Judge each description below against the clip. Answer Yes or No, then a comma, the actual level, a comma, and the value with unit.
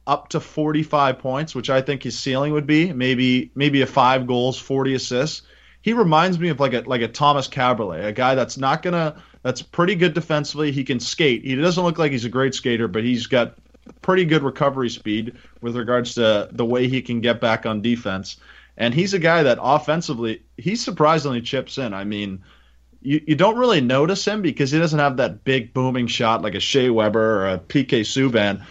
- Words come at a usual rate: No, fast, 210 wpm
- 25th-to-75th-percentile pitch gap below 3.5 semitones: No, average, 4.1 semitones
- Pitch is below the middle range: Yes, low, 130 Hz